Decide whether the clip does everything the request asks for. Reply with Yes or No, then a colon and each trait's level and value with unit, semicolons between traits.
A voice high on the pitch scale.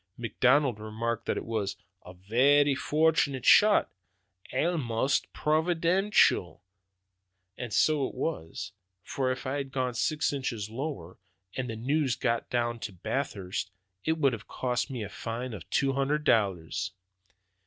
No: low, 130 Hz